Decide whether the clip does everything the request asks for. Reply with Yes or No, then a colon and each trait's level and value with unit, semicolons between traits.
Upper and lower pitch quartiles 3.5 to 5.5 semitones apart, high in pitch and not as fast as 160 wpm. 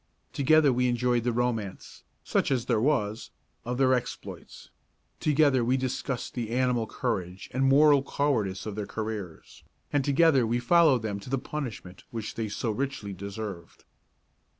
No: average, 4.0 semitones; low, 120 Hz; average, 150 wpm